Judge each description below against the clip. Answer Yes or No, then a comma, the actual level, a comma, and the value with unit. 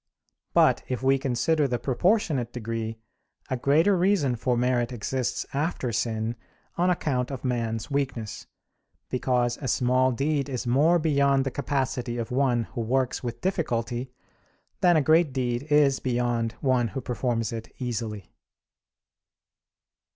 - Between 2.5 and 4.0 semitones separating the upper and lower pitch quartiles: Yes, average, 2.8 semitones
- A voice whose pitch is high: No, low, 125 Hz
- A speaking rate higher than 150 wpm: No, slow, 135 wpm